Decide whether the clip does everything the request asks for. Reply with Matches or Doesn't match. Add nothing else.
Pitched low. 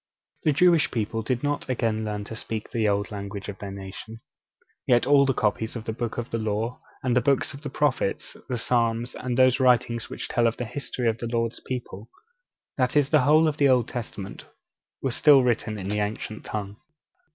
Matches